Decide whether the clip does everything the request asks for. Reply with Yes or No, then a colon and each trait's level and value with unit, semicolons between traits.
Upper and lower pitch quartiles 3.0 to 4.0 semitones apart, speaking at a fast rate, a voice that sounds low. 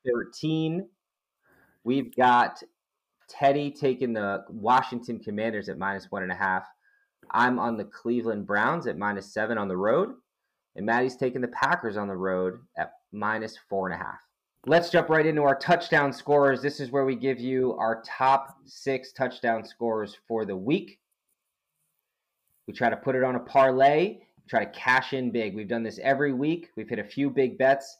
No: average, 3.7 semitones; average, 180 wpm; low, 130 Hz